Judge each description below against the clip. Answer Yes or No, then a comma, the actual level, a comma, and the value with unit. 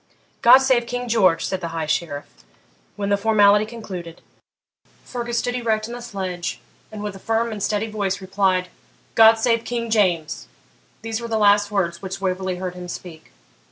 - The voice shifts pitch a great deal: No, average, 3.7 semitones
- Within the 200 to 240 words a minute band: No, average, 175 wpm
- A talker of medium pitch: No, high, 205 Hz